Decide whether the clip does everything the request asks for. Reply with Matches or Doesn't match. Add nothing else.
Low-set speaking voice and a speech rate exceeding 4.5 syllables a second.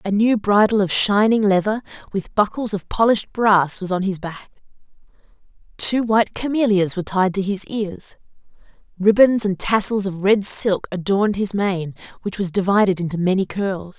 Doesn't match